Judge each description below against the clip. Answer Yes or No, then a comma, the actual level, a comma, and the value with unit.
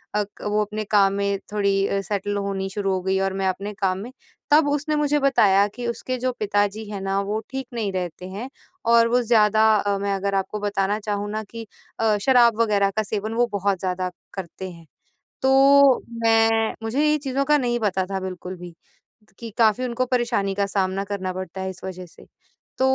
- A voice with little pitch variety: No, average, 3.2 semitones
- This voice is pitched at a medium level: No, high, 205 Hz